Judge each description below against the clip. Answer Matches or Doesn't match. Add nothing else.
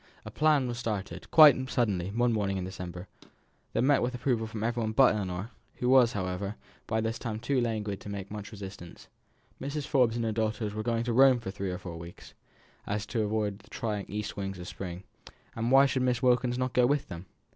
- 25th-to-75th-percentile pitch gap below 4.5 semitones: Matches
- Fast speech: Matches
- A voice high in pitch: Doesn't match